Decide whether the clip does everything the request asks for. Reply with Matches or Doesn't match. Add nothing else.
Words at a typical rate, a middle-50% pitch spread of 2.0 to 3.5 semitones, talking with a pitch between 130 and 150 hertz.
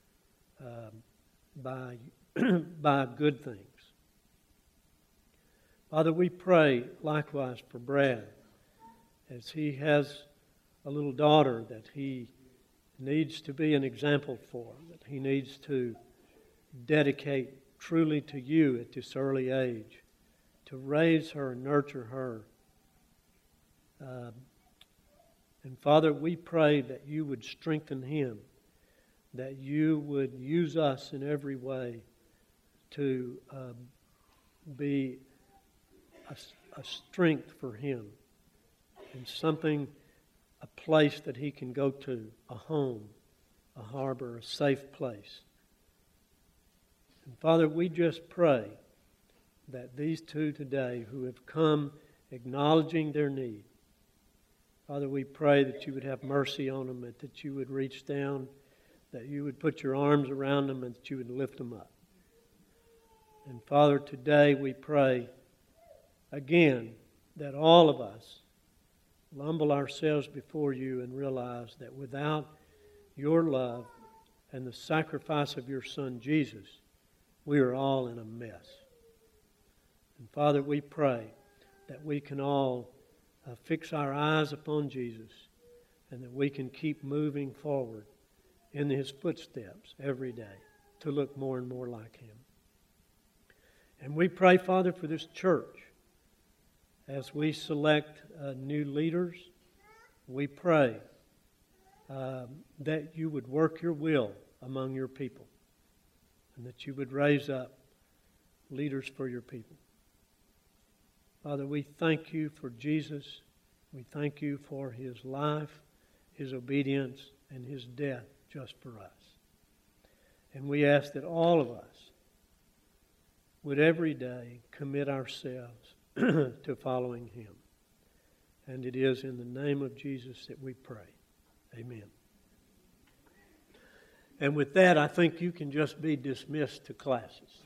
Doesn't match